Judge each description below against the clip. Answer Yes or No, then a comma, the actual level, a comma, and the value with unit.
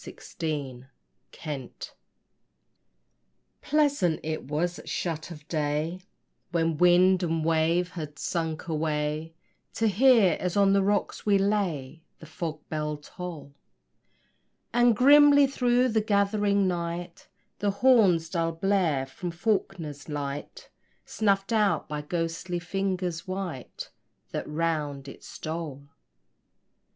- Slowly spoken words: Yes, slow, 115 wpm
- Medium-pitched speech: Yes, medium, 170 Hz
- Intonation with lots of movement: No, average, 4.3 semitones